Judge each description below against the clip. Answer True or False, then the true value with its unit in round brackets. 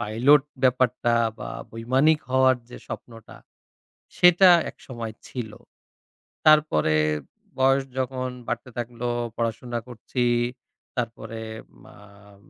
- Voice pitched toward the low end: True (120 Hz)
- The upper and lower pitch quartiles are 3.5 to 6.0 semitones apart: False (2.5 semitones)